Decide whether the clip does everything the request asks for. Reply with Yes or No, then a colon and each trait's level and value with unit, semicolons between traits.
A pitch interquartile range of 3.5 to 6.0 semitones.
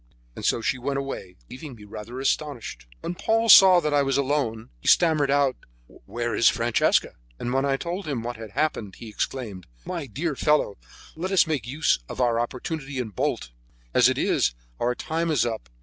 Yes: average, 4.7 semitones